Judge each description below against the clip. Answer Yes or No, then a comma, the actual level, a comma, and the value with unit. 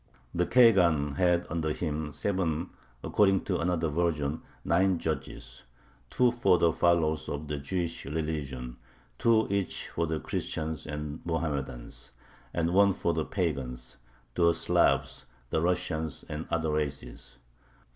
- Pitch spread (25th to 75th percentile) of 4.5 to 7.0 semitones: No, average, 2.9 semitones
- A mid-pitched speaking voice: No, very low, 80 Hz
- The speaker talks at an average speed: No, slow, 130 wpm